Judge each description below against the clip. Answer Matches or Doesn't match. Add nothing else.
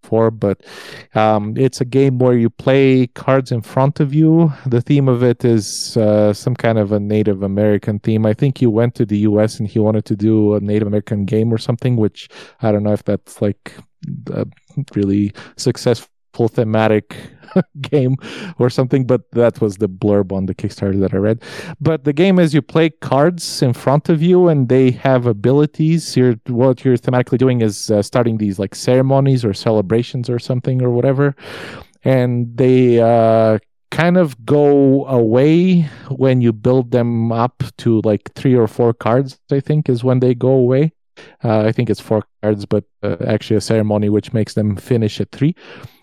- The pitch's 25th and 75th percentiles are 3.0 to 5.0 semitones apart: Matches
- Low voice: Matches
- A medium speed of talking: Matches